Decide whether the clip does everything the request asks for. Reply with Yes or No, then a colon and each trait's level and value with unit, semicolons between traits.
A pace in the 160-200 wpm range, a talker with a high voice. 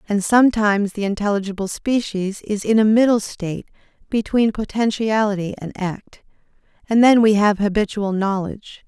No: slow, 135 wpm; high, 210 Hz